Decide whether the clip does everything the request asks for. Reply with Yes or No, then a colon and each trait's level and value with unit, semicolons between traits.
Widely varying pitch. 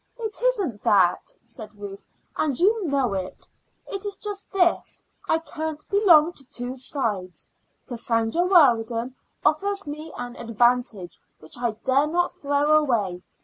Yes: wide, 7.1 semitones